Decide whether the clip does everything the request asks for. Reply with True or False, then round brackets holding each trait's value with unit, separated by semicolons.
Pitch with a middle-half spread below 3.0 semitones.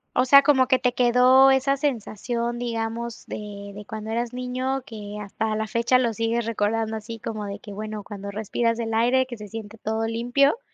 True (2.6 semitones)